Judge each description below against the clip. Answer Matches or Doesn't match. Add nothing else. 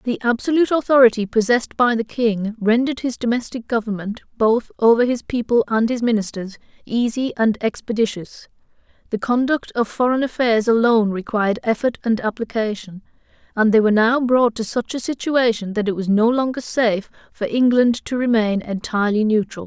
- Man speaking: Doesn't match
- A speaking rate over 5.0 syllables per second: Matches